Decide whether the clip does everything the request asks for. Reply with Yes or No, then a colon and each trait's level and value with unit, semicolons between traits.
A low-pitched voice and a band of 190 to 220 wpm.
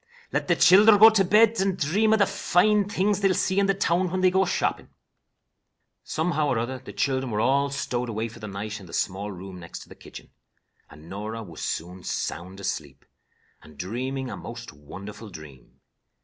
Yes: low, 125 Hz; average, 195 wpm